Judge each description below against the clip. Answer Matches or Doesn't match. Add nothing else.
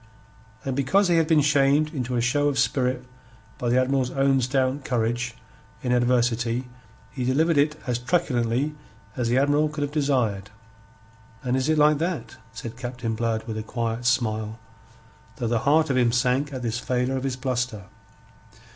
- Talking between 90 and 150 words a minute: Doesn't match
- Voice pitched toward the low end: Matches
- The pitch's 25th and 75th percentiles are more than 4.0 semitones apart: Doesn't match